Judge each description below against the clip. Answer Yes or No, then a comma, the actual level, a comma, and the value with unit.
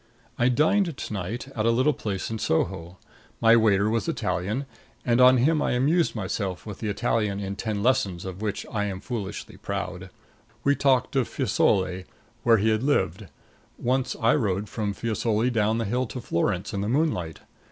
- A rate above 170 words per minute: Yes, average, 180 wpm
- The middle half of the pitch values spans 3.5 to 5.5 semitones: Yes, average, 4.2 semitones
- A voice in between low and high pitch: No, low, 110 Hz